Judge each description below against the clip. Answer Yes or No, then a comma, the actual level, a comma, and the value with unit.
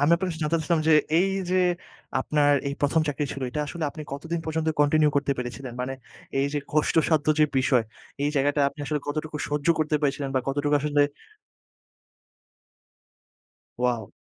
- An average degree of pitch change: No, narrow, 2.2 semitones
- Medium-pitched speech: Yes, medium, 150 Hz